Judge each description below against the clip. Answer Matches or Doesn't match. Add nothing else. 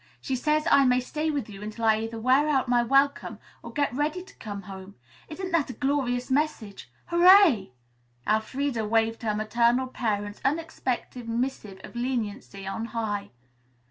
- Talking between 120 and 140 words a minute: Doesn't match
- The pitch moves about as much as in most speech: Matches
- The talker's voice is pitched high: Matches